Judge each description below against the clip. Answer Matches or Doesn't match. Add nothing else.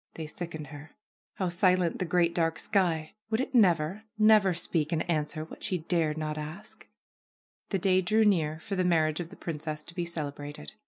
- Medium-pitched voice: Matches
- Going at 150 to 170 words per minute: Doesn't match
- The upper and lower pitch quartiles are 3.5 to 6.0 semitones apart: Doesn't match